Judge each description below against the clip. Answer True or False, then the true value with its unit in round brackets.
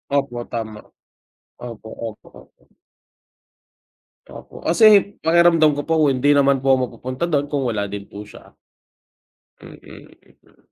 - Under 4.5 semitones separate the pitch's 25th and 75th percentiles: False (5.0 semitones)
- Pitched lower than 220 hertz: True (135 Hz)